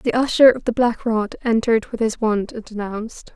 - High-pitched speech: Yes, high, 225 Hz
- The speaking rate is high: Yes, fast, 215 wpm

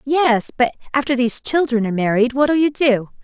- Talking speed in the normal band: Yes, average, 185 wpm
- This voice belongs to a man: No, female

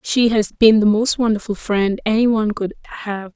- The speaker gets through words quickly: No, average, 195 wpm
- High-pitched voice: Yes, high, 215 Hz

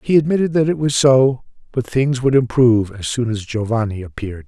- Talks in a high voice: No, low, 125 Hz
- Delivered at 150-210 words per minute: Yes, average, 200 wpm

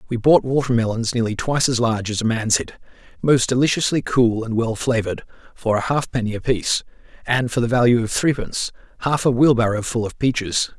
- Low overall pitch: Yes, low, 120 Hz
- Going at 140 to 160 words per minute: No, average, 185 wpm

